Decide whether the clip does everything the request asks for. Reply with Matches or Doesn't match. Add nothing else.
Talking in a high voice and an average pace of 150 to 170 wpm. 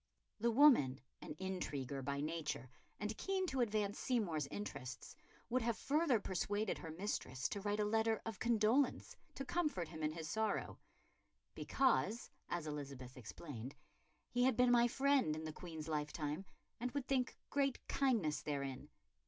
Matches